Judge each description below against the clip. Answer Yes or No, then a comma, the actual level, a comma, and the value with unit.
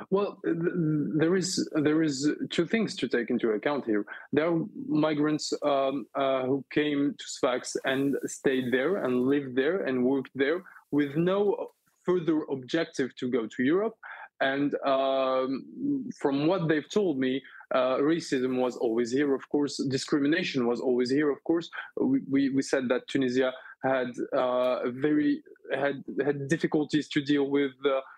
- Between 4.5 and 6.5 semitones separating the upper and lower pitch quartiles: No, average, 3.6 semitones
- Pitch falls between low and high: Yes, medium, 145 Hz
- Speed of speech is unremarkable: Yes, average, 160 wpm